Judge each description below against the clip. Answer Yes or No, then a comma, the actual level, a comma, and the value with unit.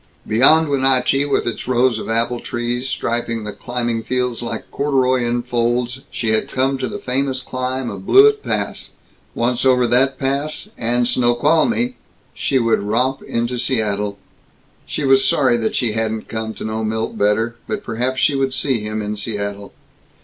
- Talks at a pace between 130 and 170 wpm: Yes, average, 165 wpm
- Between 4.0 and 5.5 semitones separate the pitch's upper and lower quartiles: No, average, 2.7 semitones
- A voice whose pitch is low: Yes, low, 125 Hz